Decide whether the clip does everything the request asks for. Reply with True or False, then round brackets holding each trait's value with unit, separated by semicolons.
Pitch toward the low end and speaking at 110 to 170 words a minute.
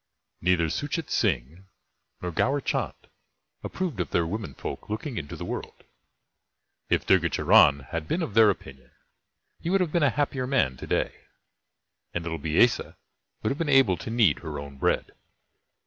True (95 Hz; 165 wpm)